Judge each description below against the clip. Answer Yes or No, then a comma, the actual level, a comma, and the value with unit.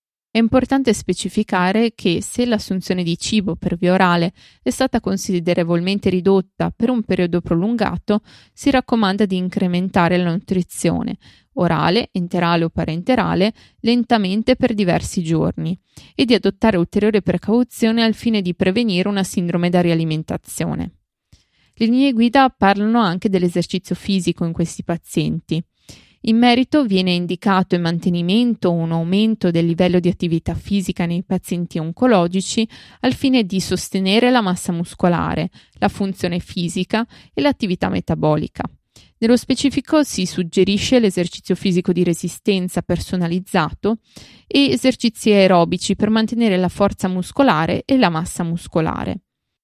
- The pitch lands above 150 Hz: Yes, high, 190 Hz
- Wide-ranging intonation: No, average, 4.1 semitones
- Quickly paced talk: No, average, 130 wpm